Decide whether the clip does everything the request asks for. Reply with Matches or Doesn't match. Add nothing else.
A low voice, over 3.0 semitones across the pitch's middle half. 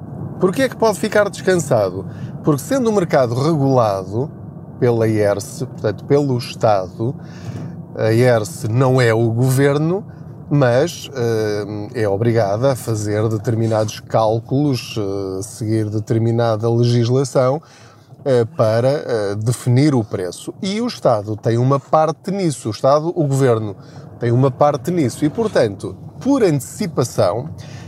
Matches